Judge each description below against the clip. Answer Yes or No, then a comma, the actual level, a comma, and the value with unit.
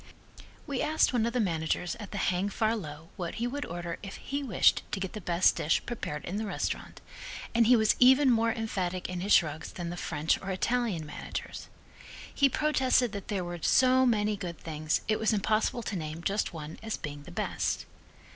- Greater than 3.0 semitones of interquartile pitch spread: Yes, average, 5.2 semitones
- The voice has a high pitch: Yes, high, 200 Hz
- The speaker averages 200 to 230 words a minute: Yes, fast, 205 wpm